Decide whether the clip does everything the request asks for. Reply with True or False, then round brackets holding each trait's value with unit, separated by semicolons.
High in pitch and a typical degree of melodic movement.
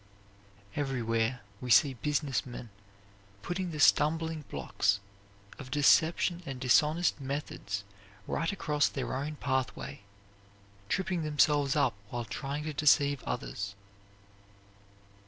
False (140 Hz; 3.5 semitones)